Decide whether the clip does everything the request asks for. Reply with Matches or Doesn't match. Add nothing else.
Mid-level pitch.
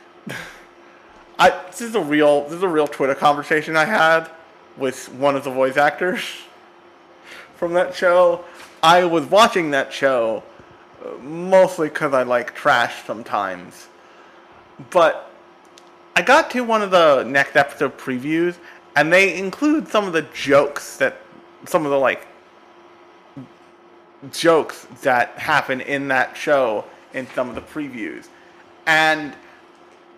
Matches